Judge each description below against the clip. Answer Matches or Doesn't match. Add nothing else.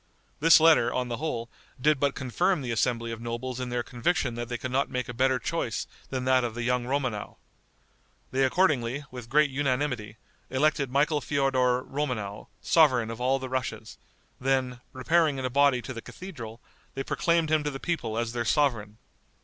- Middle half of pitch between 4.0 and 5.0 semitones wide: Doesn't match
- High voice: Doesn't match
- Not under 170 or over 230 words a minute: Matches